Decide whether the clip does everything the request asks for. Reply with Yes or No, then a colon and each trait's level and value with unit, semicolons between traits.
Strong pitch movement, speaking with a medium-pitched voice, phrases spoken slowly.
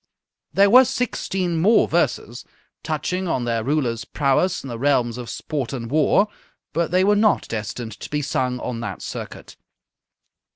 No: wide, 7.4 semitones; medium, 145 Hz; average, 165 wpm